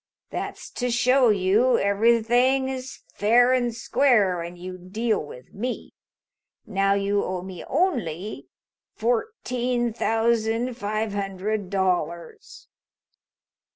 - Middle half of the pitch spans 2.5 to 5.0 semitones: Yes, average, 4.1 semitones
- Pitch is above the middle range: Yes, high, 220 Hz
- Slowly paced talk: Yes, slow, 105 wpm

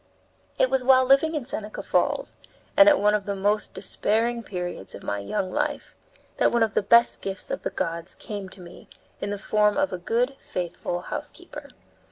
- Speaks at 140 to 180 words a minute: No, average, 195 wpm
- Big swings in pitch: No, average, 4.6 semitones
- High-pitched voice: Yes, high, 210 Hz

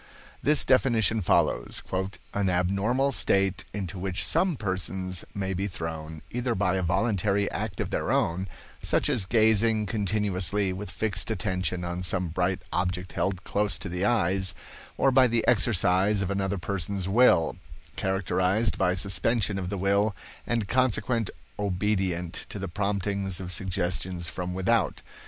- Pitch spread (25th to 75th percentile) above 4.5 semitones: No, narrow, 2.6 semitones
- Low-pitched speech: Yes, very low, 95 Hz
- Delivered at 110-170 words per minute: Yes, average, 145 wpm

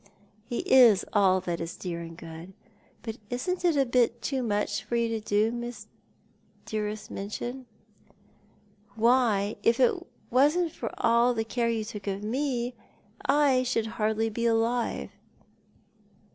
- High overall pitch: Yes, high, 230 Hz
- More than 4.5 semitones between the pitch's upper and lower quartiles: No, average, 2.9 semitones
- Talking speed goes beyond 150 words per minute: No, average, 145 wpm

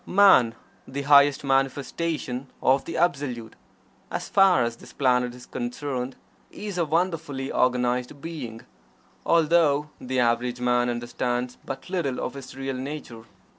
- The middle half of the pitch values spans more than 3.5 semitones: No, average, 3.2 semitones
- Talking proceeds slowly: Yes, slow, 130 wpm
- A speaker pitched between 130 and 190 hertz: Yes, low, 135 Hz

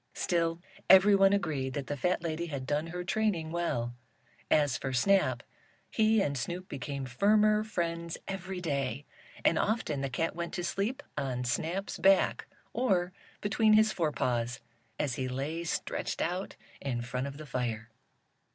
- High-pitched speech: No, medium, 165 Hz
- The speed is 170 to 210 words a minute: No, average, 150 wpm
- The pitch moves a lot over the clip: Yes, wide, 6.2 semitones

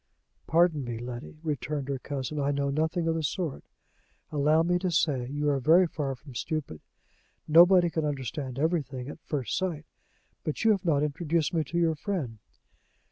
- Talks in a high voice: No, medium, 150 Hz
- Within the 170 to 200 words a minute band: Yes, average, 175 wpm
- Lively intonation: No, average, 3.3 semitones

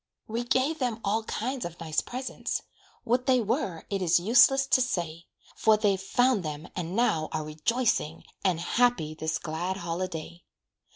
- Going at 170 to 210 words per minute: No, average, 160 wpm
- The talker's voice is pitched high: Yes, high, 195 Hz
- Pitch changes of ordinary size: No, wide, 6.7 semitones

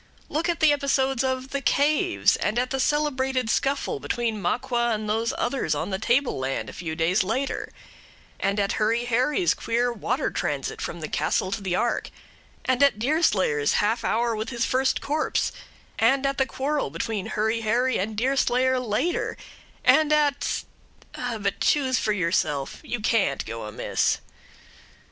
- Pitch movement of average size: Yes, average, 4.2 semitones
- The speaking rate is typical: Yes, average, 160 wpm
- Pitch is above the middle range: Yes, high, 240 Hz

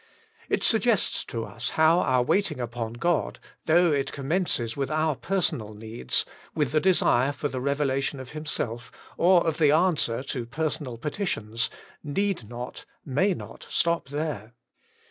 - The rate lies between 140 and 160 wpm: Yes, average, 145 wpm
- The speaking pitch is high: No, medium, 140 Hz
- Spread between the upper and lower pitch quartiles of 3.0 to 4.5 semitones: No, average, 5.2 semitones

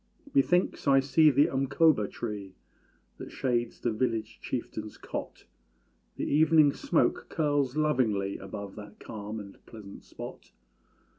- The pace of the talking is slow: Yes, slow, 125 wpm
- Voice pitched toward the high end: No, low, 120 Hz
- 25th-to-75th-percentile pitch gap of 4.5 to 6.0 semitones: Yes, wide, 5.4 semitones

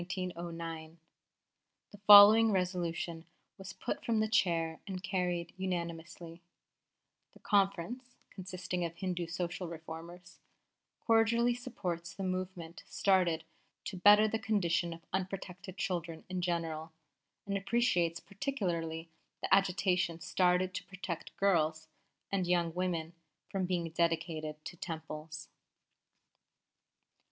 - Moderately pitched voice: Yes, medium, 180 Hz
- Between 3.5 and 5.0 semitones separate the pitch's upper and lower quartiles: No, narrow, 2.6 semitones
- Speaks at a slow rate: Yes, slow, 110 wpm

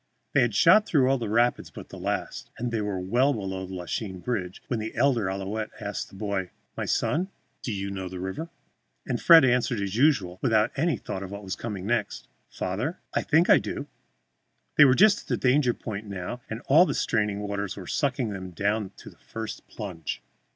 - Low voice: Yes, low, 110 Hz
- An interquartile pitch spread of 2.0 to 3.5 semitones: No, average, 4.8 semitones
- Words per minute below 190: No, fast, 205 wpm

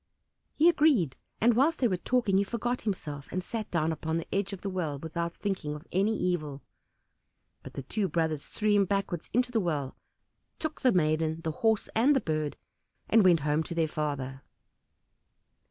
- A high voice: No, medium, 180 Hz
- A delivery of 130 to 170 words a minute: No, average, 185 wpm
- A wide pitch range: Yes, wide, 5.9 semitones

